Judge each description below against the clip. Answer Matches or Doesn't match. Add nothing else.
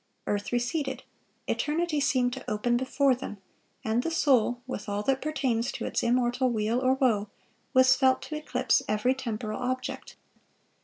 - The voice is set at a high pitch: Matches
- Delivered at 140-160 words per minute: Matches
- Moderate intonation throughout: Doesn't match